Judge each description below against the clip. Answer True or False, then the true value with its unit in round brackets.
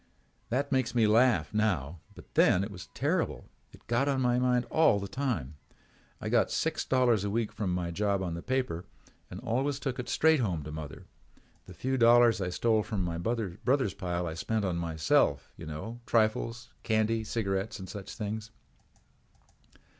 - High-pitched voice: False (110 Hz)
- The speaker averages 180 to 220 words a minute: True (185 wpm)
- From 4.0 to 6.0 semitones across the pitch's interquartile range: True (4.9 semitones)